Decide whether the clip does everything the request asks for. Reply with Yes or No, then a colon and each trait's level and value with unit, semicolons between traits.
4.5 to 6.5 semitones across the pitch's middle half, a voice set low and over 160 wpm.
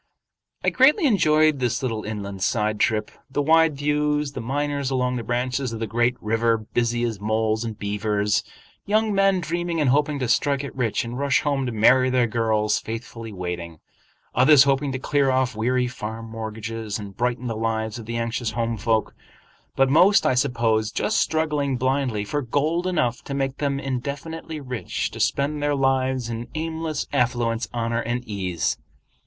No: average, 4.1 semitones; low, 125 Hz; average, 170 wpm